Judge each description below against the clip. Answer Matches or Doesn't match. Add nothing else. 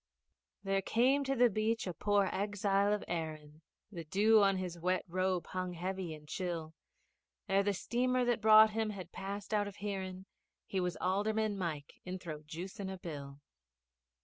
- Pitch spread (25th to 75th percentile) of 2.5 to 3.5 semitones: Matches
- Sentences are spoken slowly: Doesn't match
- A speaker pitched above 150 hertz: Matches